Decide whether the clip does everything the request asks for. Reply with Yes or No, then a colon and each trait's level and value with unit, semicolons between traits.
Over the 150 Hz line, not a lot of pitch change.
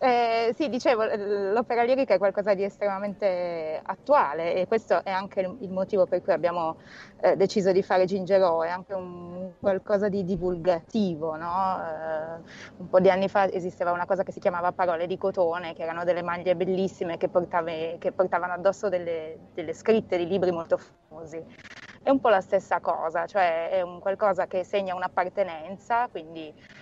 Yes: medium, 185 Hz; narrow, 2.3 semitones